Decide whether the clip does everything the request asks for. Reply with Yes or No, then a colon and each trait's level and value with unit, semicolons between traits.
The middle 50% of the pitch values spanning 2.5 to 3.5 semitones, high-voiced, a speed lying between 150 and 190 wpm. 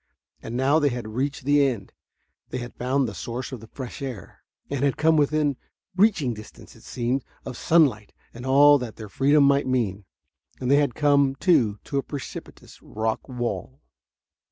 No: average, 3.1 semitones; low, 130 Hz; average, 175 wpm